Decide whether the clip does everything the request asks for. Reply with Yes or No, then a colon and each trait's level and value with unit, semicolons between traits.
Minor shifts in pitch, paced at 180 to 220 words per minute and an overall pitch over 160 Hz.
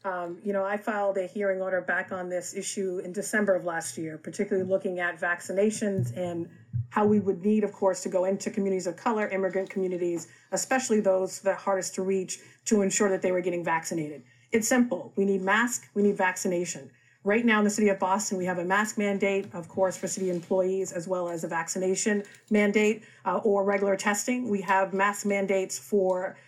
Yes: narrow, 2.1 semitones; average, 200 wpm; high, 190 Hz